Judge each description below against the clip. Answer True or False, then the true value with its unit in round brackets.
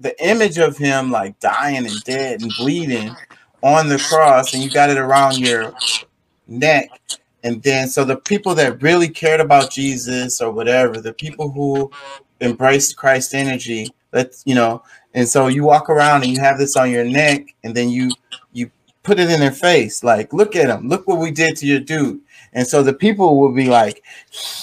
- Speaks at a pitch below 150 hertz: True (135 Hz)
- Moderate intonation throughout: True (3.1 semitones)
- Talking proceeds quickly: False (195 wpm)